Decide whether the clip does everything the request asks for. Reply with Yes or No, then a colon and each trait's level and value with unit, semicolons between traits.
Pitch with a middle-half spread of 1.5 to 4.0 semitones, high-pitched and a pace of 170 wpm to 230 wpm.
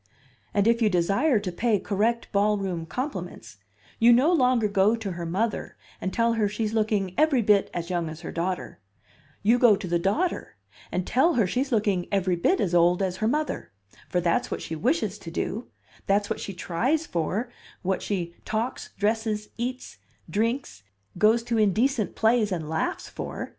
No: average, 4.4 semitones; high, 210 Hz; average, 180 wpm